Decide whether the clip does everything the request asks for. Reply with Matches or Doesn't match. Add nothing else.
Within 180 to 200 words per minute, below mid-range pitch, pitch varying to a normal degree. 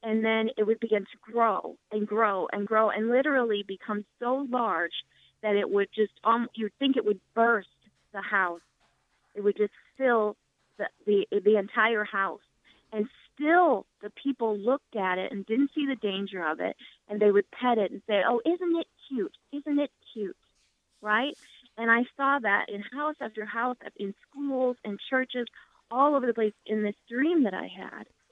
Doesn't match